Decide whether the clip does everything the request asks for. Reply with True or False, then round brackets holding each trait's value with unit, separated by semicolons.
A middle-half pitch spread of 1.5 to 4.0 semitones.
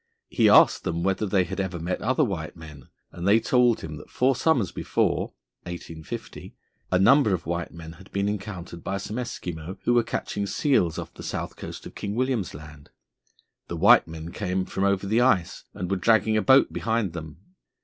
False (4.6 semitones)